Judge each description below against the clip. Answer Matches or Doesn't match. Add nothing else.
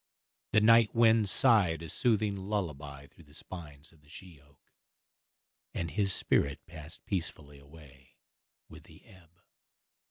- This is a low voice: Matches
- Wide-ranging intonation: Matches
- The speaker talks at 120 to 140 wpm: Matches